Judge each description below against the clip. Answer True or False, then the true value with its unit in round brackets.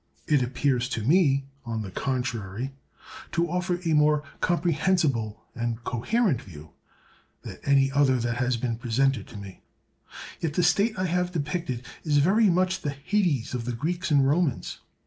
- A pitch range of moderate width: False (6.3 semitones)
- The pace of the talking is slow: False (160 wpm)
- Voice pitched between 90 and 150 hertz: True (140 Hz)